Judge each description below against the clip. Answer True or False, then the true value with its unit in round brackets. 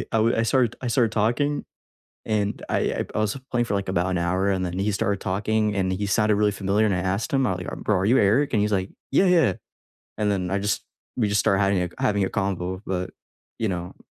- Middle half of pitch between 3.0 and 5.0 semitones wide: False (2.5 semitones)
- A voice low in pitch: True (100 Hz)